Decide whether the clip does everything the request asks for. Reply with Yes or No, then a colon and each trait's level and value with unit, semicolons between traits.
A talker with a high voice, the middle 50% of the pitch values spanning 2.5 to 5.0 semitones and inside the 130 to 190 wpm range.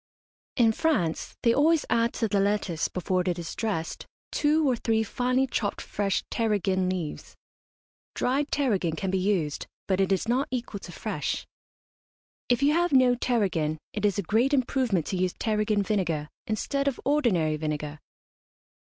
No: high, 210 Hz; wide, 5.4 semitones; average, 160 wpm